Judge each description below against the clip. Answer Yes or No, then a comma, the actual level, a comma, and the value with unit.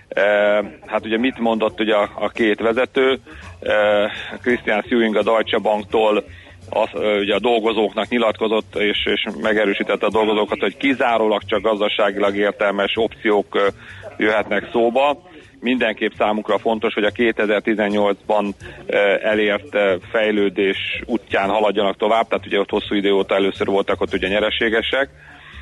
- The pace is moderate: Yes, average, 125 wpm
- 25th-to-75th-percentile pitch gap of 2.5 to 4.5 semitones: No, narrow, 1.8 semitones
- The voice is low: Yes, low, 105 Hz